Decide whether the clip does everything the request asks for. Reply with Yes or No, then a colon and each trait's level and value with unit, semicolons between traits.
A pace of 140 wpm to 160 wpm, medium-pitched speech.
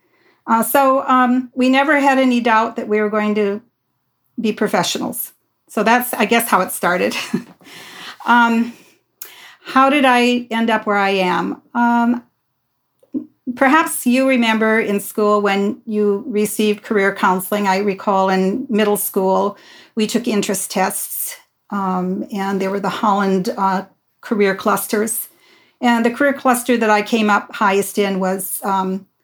No: average, 150 wpm; high, 220 Hz